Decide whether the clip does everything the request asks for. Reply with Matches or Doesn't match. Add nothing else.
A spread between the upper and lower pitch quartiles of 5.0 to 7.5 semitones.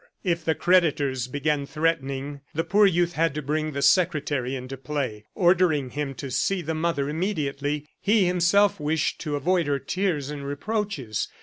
Doesn't match